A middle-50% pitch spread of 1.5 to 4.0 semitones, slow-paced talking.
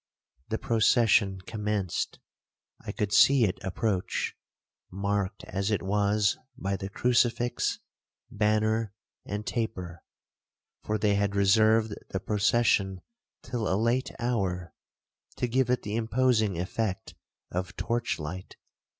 Yes: average, 2.8 semitones; slow, 115 wpm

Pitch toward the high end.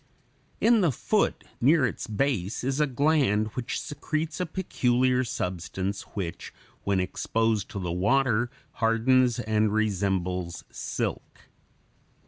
No: low, 115 Hz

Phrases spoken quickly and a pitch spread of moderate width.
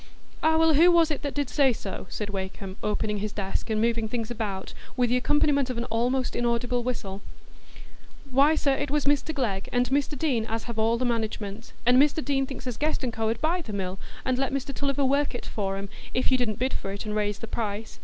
Yes: fast, 230 wpm; average, 4.5 semitones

